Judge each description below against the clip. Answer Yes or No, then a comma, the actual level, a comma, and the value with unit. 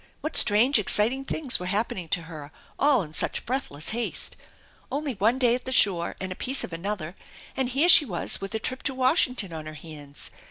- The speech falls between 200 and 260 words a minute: Yes, fast, 205 wpm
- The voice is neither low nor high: No, high, 215 Hz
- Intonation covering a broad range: Yes, wide, 7.2 semitones